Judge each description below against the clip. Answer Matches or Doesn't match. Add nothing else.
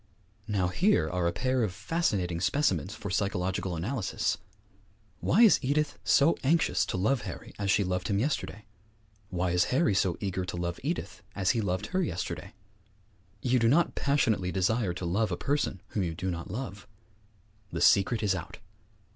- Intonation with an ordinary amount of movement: Doesn't match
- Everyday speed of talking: Matches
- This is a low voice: Matches